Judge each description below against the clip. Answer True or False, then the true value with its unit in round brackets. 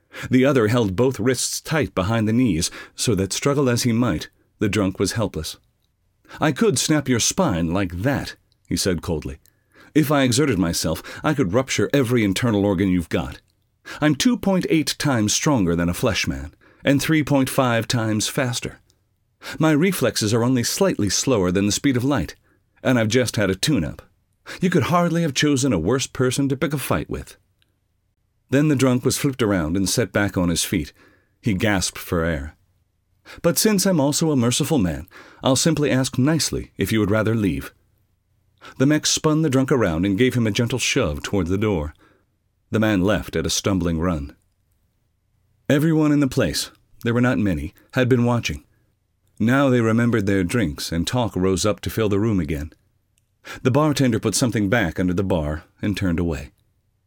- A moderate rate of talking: True (185 wpm)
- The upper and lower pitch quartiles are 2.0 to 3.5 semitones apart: False (5.5 semitones)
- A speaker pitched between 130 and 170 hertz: False (110 Hz)